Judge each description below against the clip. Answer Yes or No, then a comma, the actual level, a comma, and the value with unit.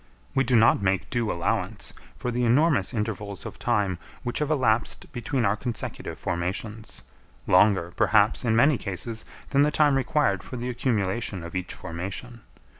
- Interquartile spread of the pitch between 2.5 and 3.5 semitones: No, average, 4.2 semitones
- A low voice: Yes, low, 110 Hz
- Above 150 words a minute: Yes, average, 160 wpm